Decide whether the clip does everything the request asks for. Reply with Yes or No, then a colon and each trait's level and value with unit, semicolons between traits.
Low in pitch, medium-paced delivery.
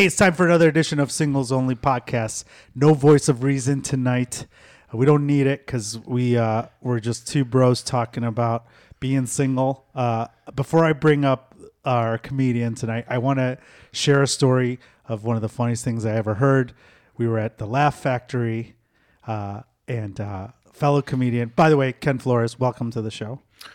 Yes: low, 125 Hz; average, 185 wpm